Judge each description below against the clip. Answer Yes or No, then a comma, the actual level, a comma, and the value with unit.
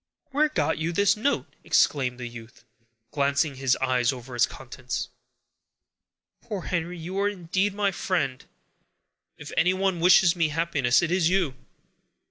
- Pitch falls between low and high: Yes, medium, 165 Hz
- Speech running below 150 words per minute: Yes, average, 140 wpm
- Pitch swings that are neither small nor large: No, wide, 6.1 semitones